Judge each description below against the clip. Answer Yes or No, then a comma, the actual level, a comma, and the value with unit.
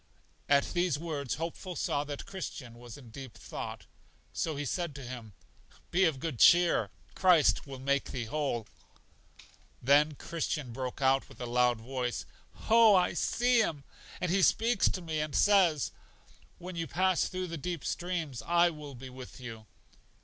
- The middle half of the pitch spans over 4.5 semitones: Yes, average, 5.3 semitones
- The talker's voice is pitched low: No, medium, 150 Hz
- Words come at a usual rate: Yes, average, 165 wpm